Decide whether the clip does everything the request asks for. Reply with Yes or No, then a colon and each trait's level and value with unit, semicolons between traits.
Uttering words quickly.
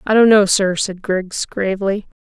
No: average, 190 wpm